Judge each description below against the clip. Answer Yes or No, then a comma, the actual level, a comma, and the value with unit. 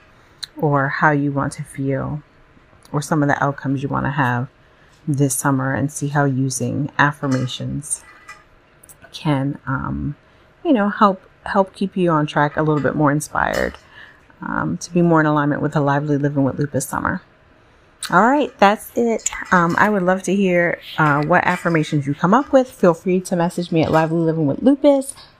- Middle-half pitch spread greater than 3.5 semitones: Yes, average, 4.2 semitones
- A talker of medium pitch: Yes, medium, 150 Hz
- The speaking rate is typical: Yes, average, 180 wpm